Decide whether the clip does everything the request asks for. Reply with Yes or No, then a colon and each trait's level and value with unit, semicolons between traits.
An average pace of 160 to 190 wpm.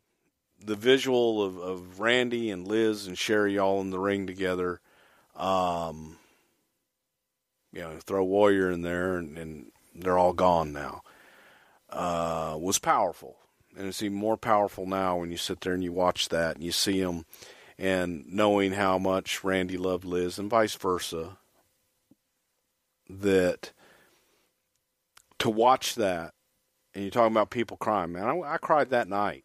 No: average, 150 wpm